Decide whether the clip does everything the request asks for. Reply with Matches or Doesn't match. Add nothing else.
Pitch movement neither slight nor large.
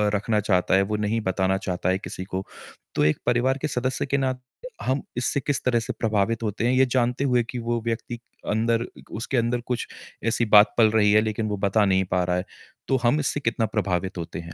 Matches